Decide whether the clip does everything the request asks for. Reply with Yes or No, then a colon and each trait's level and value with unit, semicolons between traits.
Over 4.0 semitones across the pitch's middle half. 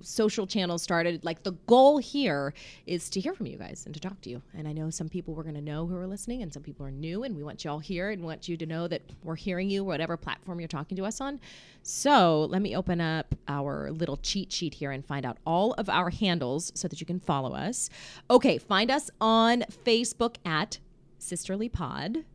Yes: average, 4.8 semitones